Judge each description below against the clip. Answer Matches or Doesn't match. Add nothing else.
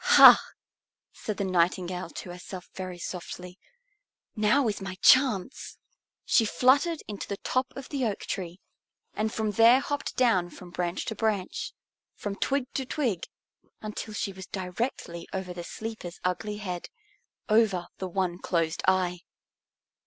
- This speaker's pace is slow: Doesn't match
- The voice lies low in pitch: Doesn't match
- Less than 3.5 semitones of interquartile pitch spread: Doesn't match